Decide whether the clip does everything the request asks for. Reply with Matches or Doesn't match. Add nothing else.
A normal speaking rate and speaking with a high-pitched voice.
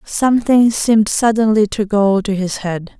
Matches